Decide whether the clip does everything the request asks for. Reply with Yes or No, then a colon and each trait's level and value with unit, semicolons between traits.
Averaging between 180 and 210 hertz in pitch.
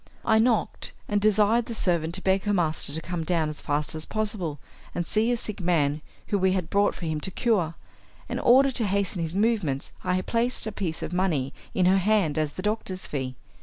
Yes: medium, 185 Hz